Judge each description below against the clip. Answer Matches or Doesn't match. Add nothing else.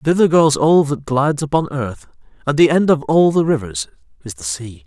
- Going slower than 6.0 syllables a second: Matches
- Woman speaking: Doesn't match